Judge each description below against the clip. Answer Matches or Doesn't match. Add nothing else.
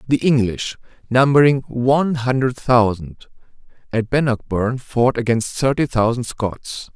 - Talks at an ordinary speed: Doesn't match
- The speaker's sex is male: Matches